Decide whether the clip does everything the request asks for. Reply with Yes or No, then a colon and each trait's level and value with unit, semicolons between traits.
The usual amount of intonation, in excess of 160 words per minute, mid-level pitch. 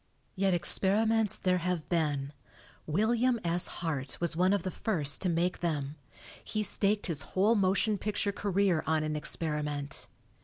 No: average, 4.6 semitones; average, 150 wpm; medium, 180 Hz